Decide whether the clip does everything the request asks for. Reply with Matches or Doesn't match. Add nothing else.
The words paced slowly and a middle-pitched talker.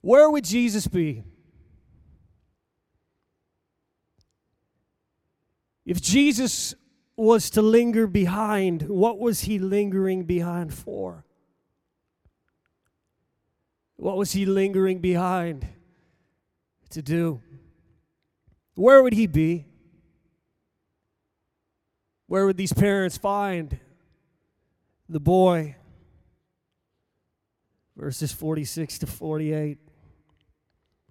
Matches